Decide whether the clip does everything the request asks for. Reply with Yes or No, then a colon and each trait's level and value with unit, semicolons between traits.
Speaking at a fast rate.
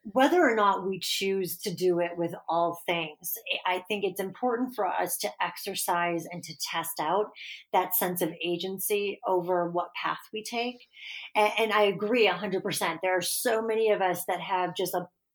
No: average, 190 wpm